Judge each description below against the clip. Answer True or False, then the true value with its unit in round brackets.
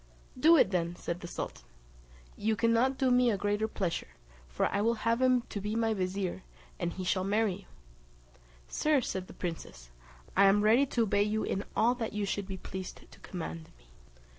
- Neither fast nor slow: True (195 wpm)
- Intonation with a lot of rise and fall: False (3.8 semitones)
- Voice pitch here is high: True (205 Hz)